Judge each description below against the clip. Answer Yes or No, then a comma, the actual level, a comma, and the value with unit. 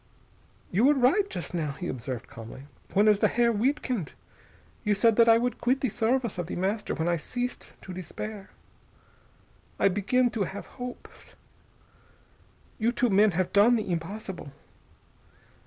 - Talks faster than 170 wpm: No, average, 155 wpm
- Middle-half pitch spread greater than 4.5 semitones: Yes, average, 5.1 semitones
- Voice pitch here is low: No, high, 210 Hz